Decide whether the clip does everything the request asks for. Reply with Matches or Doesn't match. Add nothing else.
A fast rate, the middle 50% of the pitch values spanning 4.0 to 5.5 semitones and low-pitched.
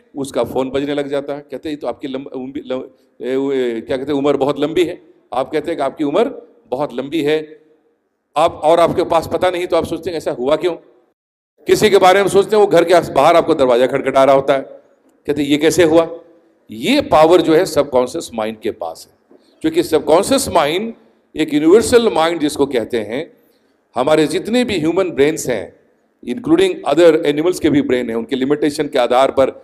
Doesn't match